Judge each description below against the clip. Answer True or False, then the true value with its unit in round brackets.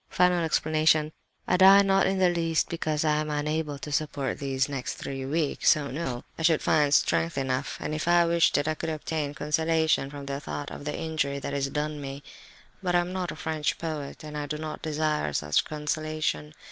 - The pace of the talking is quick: True (210 wpm)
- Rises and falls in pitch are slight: True (2.2 semitones)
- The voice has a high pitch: False (155 Hz)